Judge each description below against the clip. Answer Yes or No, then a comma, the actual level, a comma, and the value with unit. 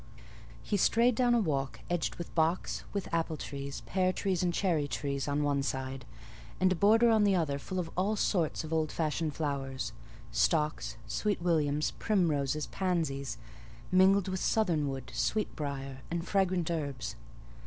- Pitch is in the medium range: Yes, medium, 165 Hz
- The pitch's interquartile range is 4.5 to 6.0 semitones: Yes, average, 4.8 semitones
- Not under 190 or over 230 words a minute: No, average, 160 wpm